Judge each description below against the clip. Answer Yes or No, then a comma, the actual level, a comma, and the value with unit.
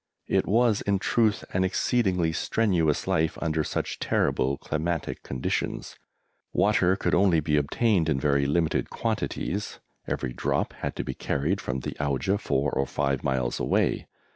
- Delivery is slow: No, average, 150 wpm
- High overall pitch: No, very low, 80 Hz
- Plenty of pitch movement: Yes, wide, 5.7 semitones